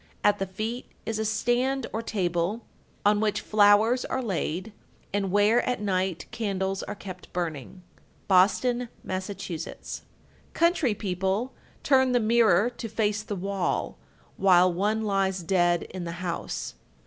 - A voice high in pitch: Yes, high, 205 Hz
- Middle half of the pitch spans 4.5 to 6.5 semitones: No, average, 3.3 semitones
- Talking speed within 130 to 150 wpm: Yes, average, 140 wpm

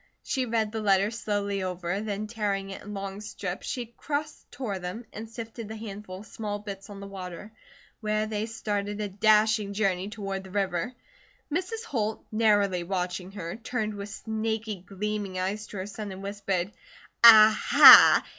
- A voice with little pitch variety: Yes, narrow, 2.0 semitones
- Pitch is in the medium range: No, high, 205 Hz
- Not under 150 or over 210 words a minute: Yes, average, 170 wpm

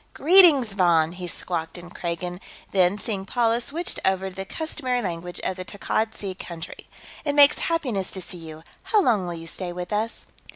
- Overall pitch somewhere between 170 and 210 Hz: Yes, high, 190 Hz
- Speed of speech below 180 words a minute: No, average, 190 wpm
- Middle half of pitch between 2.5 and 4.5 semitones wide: No, average, 5.3 semitones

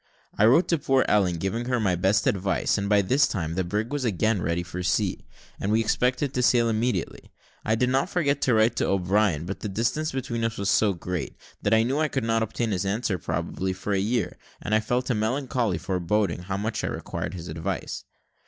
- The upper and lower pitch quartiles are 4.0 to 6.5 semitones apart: Yes, average, 4.3 semitones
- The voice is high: No, low, 110 Hz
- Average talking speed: No, fast, 220 wpm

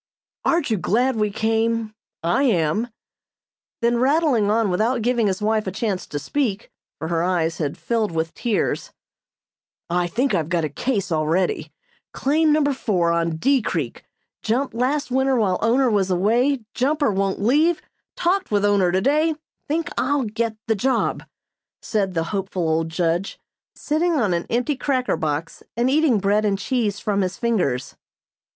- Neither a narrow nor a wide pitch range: No, wide, 6.1 semitones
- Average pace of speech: Yes, average, 160 wpm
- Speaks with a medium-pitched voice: No, high, 215 Hz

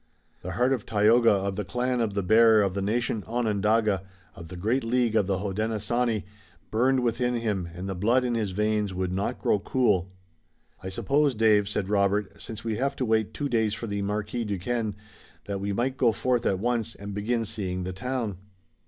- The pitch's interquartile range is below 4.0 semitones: Yes, average, 3.2 semitones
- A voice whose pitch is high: No, low, 105 Hz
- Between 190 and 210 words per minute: Yes, average, 195 wpm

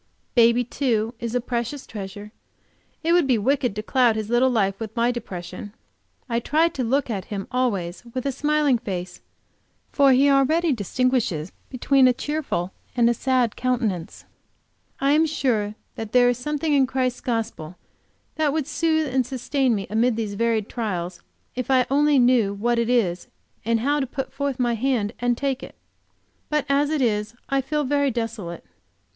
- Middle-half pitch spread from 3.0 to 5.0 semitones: Yes, average, 4.0 semitones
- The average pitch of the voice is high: Yes, high, 245 Hz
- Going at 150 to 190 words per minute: Yes, average, 175 wpm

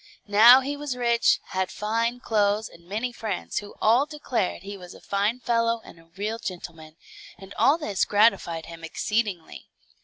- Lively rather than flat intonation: No, average, 3.9 semitones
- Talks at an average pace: Yes, average, 165 wpm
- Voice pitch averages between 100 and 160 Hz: No, high, 215 Hz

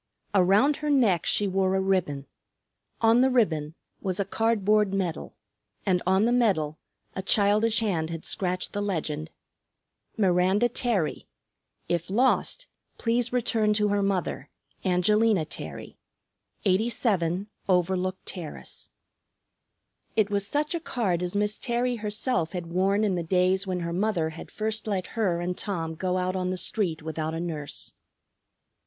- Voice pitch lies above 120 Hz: Yes, high, 190 Hz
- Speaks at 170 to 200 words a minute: No, average, 150 wpm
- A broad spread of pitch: No, average, 3.5 semitones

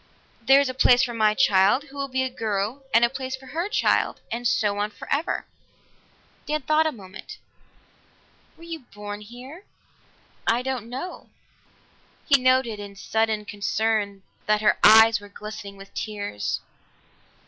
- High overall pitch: Yes, high, 230 Hz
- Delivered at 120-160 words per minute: Yes, average, 155 wpm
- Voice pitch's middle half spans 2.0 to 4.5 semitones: Yes, average, 4.1 semitones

